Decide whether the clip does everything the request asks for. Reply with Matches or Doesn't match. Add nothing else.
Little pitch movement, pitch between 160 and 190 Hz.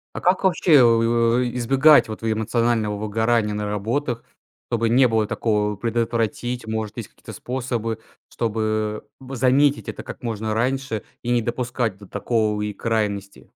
Doesn't match